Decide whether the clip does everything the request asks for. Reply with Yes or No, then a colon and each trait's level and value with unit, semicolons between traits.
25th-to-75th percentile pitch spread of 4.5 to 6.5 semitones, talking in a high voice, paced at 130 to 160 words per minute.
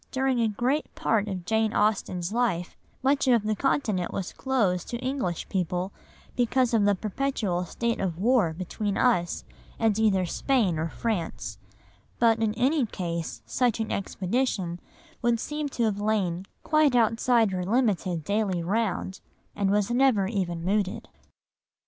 Yes: average, 4.8 semitones; high, 215 Hz; average, 150 wpm